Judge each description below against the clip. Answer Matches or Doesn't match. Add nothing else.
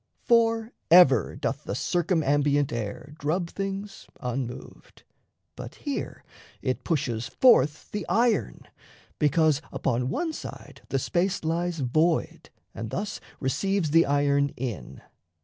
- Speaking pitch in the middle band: Matches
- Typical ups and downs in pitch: Doesn't match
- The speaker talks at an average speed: Doesn't match